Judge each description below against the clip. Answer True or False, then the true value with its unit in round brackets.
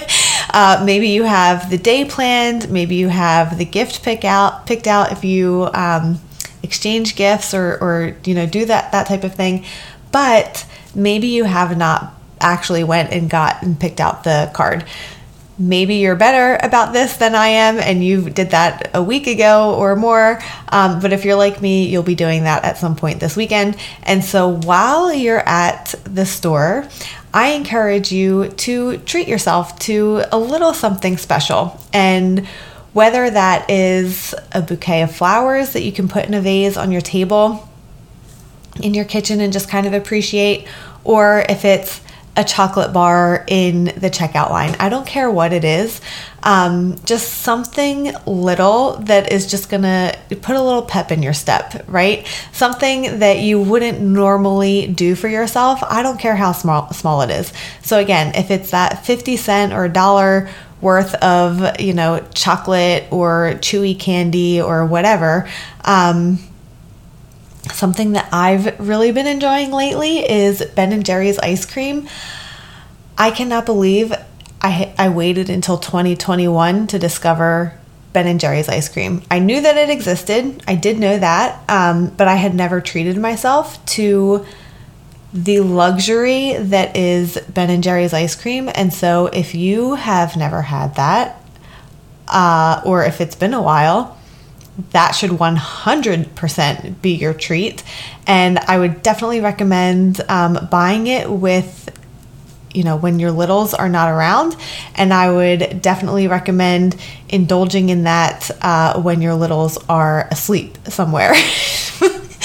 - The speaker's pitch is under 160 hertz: False (185 Hz)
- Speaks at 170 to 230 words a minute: False (160 wpm)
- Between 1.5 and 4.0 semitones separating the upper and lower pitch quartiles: True (3.3 semitones)